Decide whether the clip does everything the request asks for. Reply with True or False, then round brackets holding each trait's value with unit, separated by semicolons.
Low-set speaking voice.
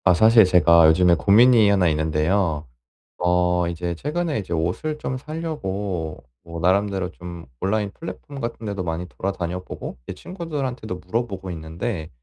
True (95 Hz)